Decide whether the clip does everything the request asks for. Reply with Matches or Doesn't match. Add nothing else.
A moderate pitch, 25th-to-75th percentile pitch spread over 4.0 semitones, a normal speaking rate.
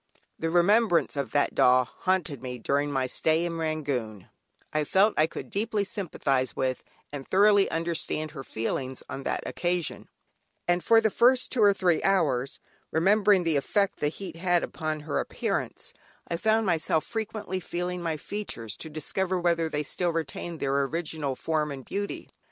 Matches